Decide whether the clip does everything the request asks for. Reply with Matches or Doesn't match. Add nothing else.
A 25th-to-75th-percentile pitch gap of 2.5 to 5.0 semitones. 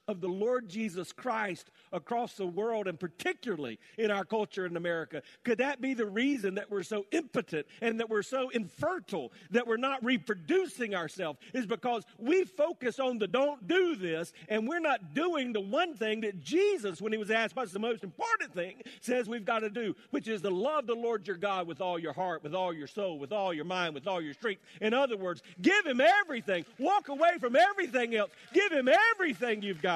Doesn't match